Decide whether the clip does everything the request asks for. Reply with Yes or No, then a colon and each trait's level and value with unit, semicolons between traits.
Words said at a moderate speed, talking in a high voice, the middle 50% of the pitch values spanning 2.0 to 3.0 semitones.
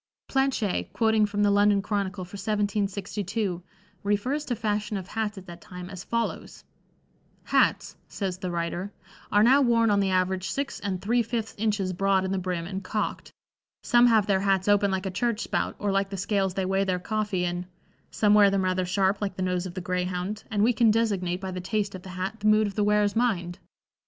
No: fast, 210 wpm; high, 200 Hz; narrow, 2.4 semitones